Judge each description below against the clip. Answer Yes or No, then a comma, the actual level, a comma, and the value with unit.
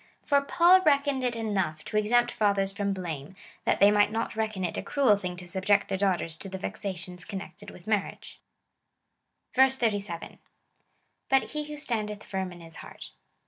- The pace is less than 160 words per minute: No, average, 185 wpm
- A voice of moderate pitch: No, high, 205 Hz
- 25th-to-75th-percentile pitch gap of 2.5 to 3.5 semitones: No, average, 4.4 semitones